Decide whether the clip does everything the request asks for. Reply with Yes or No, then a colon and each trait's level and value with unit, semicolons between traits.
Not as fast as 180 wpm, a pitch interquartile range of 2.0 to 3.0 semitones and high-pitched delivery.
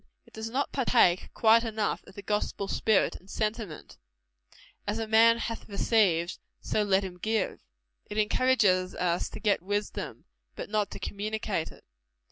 Yes: average, 155 wpm; narrow, 2.6 semitones; high, 210 Hz